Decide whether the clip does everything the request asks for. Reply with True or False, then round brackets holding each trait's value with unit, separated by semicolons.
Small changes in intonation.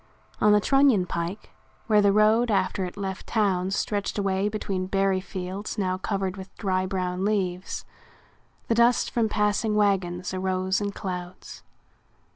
True (2.1 semitones)